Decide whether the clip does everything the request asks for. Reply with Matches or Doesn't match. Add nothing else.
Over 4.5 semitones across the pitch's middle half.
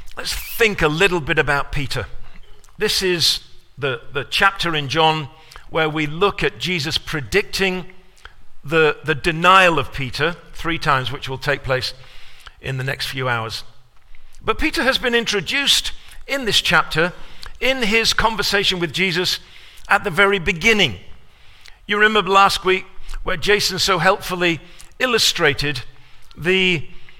Matches